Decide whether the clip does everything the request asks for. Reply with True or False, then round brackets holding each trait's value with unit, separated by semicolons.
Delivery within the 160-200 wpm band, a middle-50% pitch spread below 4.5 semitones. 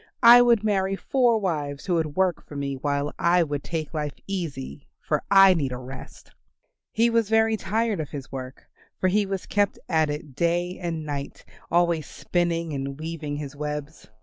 False (180 wpm; 5.0 semitones)